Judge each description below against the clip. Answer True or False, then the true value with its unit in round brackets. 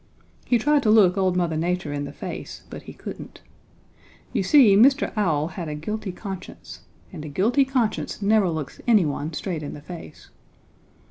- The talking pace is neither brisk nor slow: True (175 wpm)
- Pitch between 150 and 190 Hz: True (185 Hz)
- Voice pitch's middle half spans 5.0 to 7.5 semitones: True (5.5 semitones)